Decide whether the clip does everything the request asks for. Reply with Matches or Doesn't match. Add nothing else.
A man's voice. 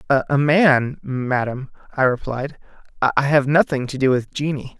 Matches